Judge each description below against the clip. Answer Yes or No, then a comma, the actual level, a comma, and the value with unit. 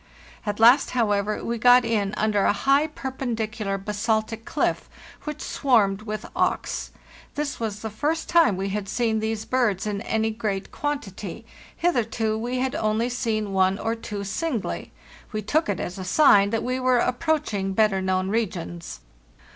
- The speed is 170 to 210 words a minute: No, average, 160 wpm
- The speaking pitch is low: No, high, 220 Hz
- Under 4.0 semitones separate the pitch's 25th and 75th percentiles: Yes, average, 3.6 semitones